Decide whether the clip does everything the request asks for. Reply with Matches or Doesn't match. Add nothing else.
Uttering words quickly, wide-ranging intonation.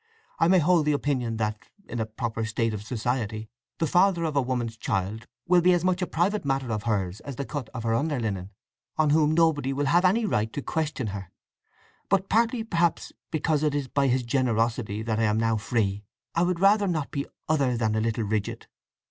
Matches